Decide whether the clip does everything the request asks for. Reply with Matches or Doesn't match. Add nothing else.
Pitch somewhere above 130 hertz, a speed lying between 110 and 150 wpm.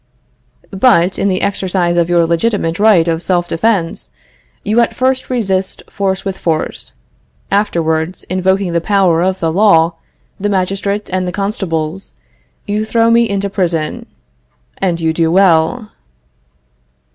Matches